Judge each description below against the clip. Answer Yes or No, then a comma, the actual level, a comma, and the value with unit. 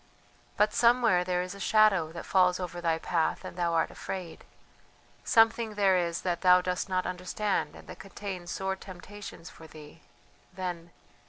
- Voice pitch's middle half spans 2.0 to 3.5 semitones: Yes, narrow, 2.4 semitones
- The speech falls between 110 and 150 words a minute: No, average, 165 wpm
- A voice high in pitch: No, medium, 180 Hz